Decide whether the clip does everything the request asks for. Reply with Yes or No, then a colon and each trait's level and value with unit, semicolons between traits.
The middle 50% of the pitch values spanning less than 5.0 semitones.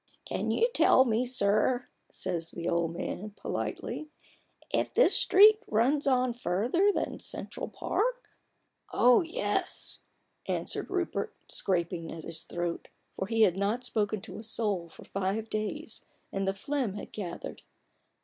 No: average, 5.3 semitones